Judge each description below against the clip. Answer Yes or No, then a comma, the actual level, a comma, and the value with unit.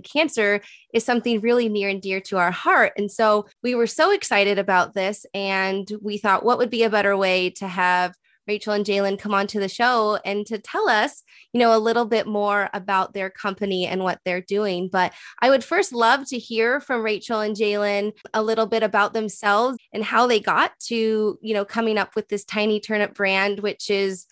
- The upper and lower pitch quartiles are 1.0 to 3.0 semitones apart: Yes, narrow, 2.4 semitones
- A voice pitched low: No, high, 210 Hz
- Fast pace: Yes, fast, 210 wpm